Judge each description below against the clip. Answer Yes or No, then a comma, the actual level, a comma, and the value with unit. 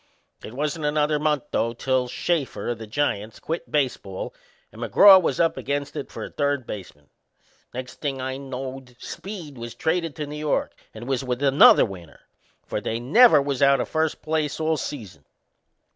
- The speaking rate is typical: Yes, average, 175 wpm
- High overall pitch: No, medium, 140 Hz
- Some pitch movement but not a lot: Yes, average, 4.0 semitones